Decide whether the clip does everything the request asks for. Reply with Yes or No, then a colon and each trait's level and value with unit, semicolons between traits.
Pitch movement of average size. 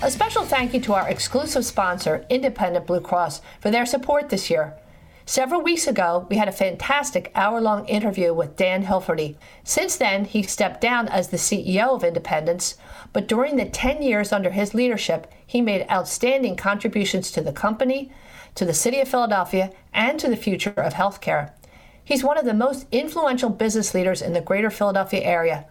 No: wide, 5.7 semitones